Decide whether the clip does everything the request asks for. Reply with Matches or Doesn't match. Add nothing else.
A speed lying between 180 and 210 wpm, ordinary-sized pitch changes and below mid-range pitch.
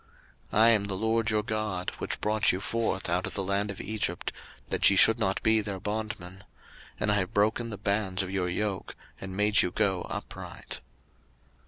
Doesn't match